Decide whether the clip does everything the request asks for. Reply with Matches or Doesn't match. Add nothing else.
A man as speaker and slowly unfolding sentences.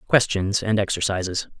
Matches